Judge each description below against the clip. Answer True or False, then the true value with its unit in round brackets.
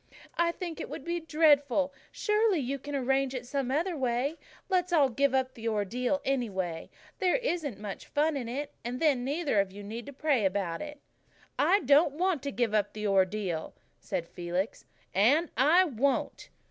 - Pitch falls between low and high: False (270 Hz)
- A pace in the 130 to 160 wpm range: False (175 wpm)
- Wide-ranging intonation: True (5.8 semitones)